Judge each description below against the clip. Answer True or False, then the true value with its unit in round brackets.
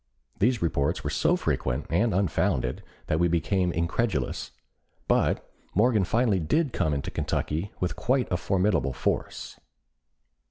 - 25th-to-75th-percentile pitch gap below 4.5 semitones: False (5.4 semitones)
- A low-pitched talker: True (90 Hz)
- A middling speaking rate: False (130 wpm)